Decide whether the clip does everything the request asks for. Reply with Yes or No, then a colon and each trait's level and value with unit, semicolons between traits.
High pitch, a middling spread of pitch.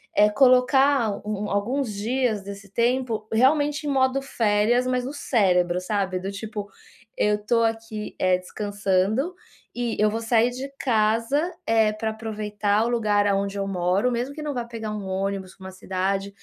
Yes: high, 215 Hz; average, 3.6 semitones